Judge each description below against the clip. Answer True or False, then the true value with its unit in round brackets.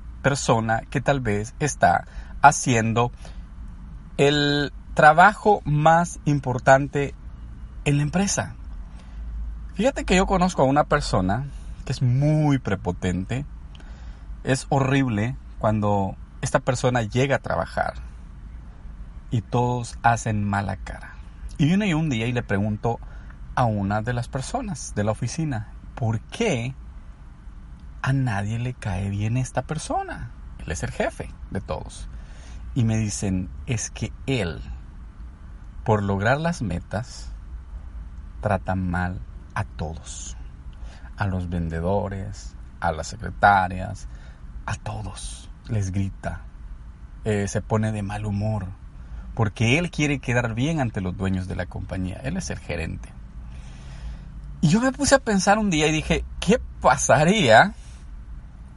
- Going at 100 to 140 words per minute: True (125 wpm)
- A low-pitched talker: True (100 Hz)